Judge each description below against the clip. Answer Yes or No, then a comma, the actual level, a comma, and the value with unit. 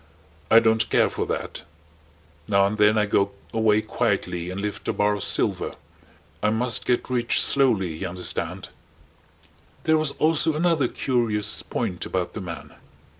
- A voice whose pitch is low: Yes, low, 105 Hz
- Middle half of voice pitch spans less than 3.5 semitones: No, average, 3.9 semitones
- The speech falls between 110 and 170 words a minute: Yes, average, 155 wpm